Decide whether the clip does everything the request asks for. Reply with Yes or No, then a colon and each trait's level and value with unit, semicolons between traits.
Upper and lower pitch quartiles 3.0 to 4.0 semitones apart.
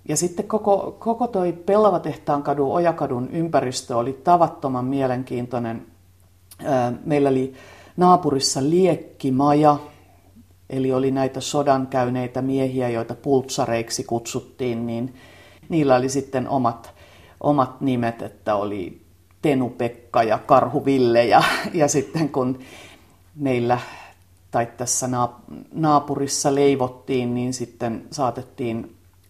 Yes: average, 3.5 semitones